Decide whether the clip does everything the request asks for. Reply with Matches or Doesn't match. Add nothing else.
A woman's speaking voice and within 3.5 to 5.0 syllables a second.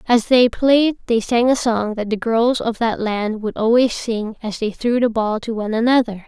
Matches